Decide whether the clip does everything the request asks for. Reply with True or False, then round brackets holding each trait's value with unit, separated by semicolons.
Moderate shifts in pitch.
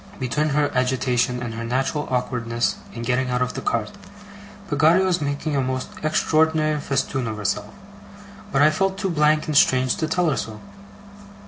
True (3.7 semitones)